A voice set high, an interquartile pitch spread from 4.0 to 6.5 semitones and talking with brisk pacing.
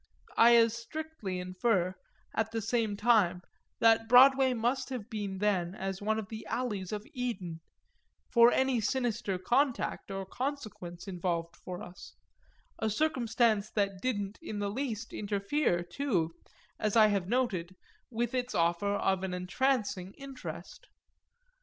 No: high, 215 Hz; average, 4.4 semitones; average, 140 wpm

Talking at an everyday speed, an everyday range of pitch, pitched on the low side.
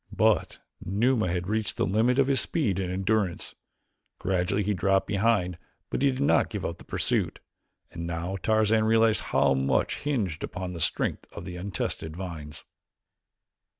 Yes: average, 160 wpm; average, 3.9 semitones; very low, 95 Hz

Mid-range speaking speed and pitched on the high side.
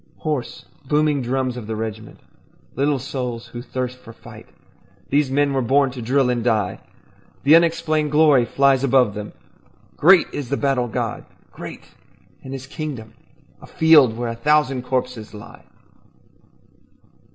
No: average, 145 wpm; low, 130 Hz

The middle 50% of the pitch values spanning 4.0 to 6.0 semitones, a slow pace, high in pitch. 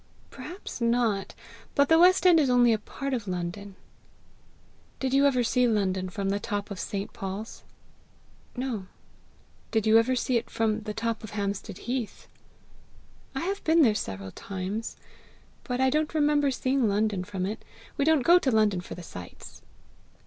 No: average, 4.8 semitones; average, 170 wpm; high, 225 Hz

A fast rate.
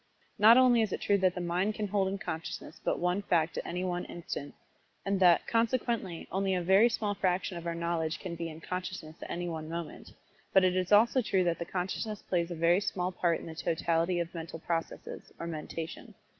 Yes: fast, 220 wpm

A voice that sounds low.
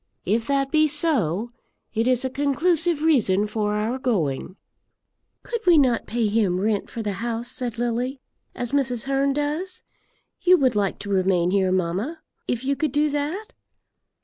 No: high, 245 Hz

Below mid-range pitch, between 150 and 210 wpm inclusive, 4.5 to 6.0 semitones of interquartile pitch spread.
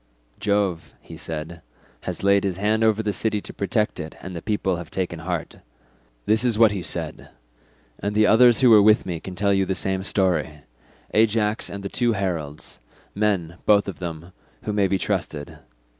No: low, 100 Hz; average, 185 wpm; average, 3.7 semitones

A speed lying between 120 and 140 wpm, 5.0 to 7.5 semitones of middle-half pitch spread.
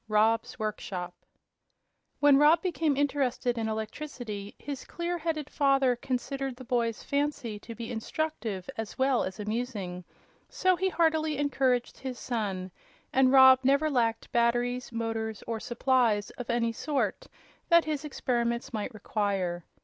No: slow, 135 wpm; average, 4.1 semitones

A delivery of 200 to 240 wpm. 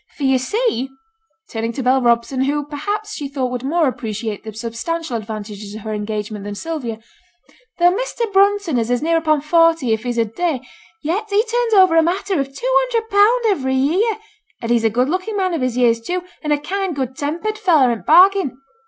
Yes: fast, 205 wpm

